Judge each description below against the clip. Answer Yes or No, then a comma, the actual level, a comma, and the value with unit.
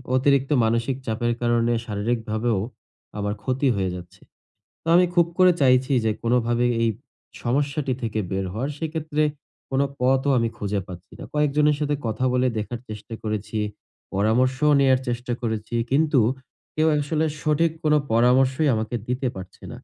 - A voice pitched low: Yes, low, 125 Hz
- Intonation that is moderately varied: Yes, average, 4.3 semitones